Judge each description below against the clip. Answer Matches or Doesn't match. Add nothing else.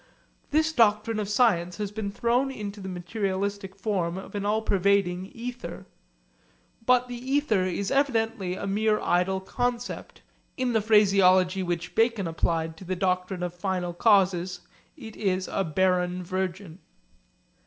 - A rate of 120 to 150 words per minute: Matches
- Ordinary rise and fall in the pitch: Matches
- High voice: Matches